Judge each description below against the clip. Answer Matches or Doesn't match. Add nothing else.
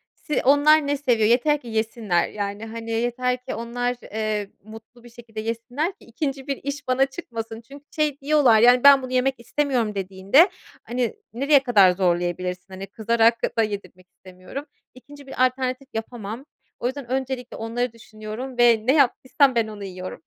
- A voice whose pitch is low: Doesn't match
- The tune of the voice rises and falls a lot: Doesn't match